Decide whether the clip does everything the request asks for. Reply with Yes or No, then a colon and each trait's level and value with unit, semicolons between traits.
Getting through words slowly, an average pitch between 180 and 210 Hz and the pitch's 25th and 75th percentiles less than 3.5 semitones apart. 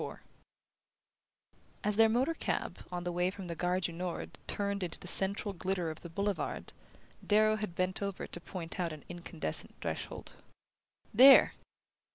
No: average, 160 wpm; medium, 185 Hz; average, 2.8 semitones